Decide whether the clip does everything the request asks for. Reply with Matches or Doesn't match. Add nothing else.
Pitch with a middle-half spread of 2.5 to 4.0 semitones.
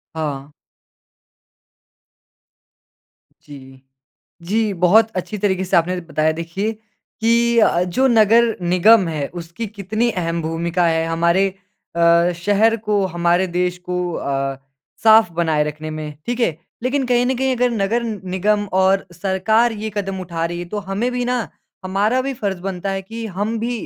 Doesn't match